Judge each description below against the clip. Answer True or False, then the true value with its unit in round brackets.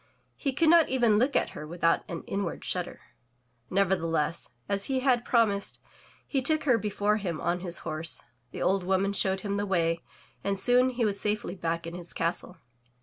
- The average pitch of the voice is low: False (200 Hz)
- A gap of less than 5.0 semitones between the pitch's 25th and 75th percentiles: False (5.4 semitones)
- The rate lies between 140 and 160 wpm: False (185 wpm)